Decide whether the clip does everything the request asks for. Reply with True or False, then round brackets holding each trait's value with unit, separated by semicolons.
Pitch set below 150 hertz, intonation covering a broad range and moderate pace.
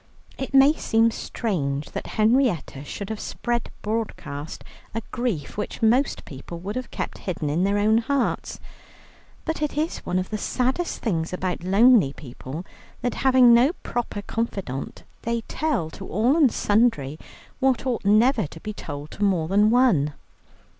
False (215 Hz; 6.5 semitones; 155 wpm)